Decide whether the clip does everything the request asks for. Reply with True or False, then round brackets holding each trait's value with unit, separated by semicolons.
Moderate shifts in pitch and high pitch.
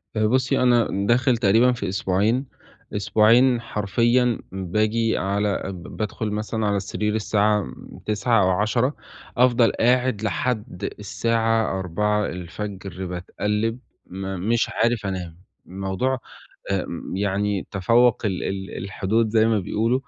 False (3.2 semitones; 105 Hz)